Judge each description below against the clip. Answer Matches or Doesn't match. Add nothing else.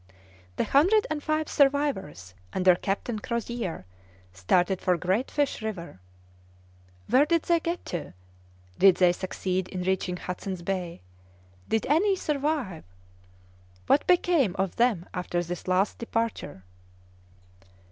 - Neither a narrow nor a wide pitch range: Doesn't match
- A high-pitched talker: Matches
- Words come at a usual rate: Doesn't match